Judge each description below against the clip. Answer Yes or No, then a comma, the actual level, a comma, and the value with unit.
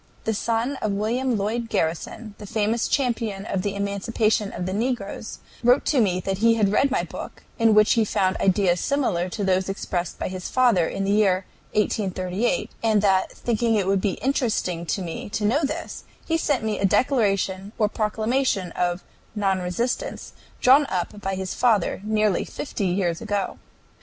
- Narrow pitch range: No, average, 3.4 semitones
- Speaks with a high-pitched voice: Yes, high, 210 Hz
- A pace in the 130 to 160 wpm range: No, average, 175 wpm